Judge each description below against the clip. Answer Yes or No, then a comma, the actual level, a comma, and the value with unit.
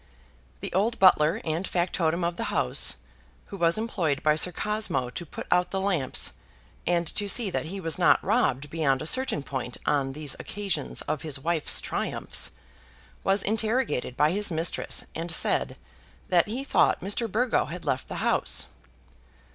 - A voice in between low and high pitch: Yes, medium, 175 Hz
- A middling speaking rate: Yes, average, 165 wpm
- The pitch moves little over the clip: No, average, 5.0 semitones